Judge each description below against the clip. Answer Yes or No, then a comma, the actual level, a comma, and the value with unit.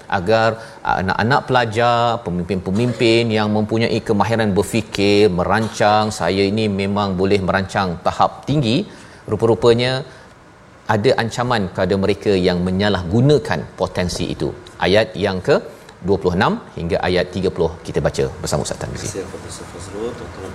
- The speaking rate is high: No, average, 105 wpm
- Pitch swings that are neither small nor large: Yes, average, 3.1 semitones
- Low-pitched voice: Yes, low, 105 Hz